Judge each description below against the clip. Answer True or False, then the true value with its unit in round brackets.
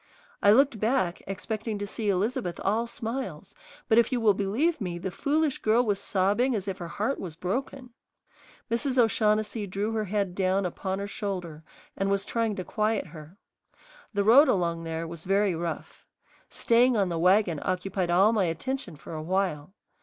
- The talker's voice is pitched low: False (200 Hz)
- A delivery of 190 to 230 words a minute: False (175 wpm)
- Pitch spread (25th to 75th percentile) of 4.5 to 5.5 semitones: False (3.8 semitones)